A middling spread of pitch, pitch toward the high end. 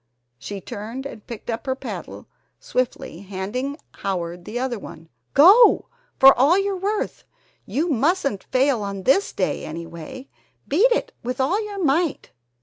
No: wide, 8.1 semitones; very high, 260 Hz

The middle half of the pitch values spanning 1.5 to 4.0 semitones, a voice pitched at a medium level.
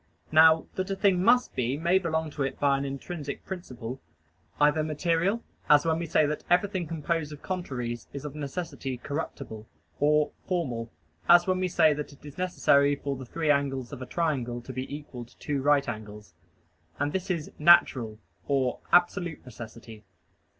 No: average, 4.5 semitones; medium, 150 Hz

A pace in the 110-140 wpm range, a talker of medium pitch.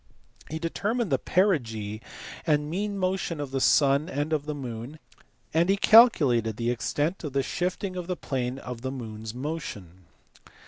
No: average, 170 wpm; medium, 145 Hz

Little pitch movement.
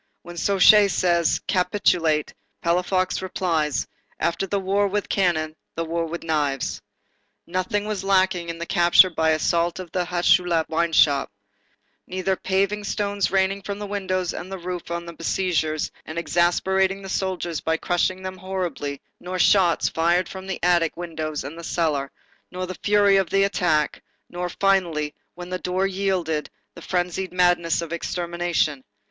Yes: narrow, 2.3 semitones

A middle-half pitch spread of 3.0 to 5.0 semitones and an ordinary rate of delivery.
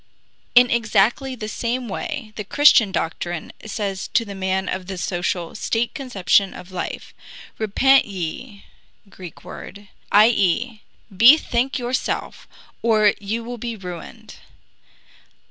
No: average, 4.0 semitones; slow, 125 wpm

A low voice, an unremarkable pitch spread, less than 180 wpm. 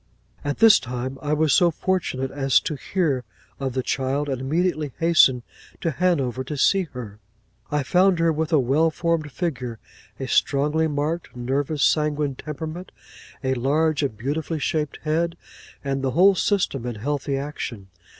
No: medium, 145 Hz; average, 3.5 semitones; average, 160 wpm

